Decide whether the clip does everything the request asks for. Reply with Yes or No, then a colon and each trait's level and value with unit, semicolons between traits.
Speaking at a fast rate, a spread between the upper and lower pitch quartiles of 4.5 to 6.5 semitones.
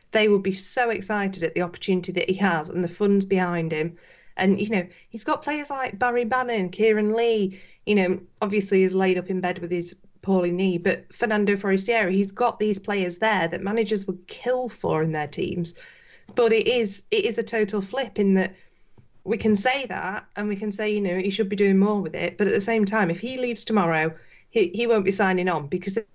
No: fast, 225 wpm; average, 3.3 semitones